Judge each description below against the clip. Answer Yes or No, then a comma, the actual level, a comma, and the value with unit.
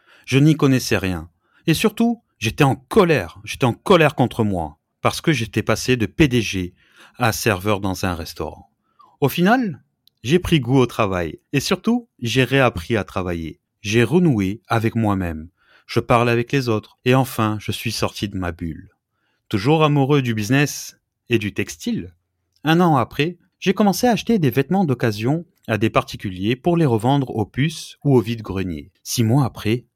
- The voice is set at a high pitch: No, low, 120 Hz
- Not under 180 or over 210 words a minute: No, average, 170 wpm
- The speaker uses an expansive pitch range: Yes, wide, 5.9 semitones